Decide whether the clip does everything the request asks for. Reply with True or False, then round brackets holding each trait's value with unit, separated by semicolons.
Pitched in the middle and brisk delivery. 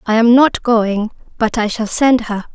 False (225 Hz; 215 wpm)